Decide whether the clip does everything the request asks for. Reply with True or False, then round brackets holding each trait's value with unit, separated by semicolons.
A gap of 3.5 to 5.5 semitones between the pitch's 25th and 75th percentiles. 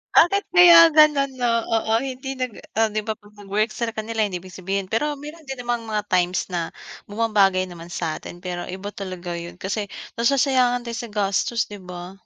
True (4.8 semitones)